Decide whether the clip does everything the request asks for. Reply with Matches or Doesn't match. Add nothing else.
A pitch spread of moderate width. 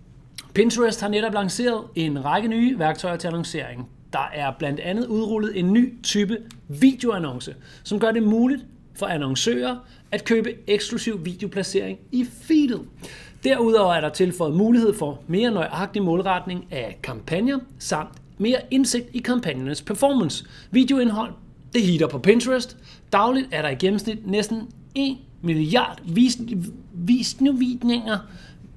Doesn't match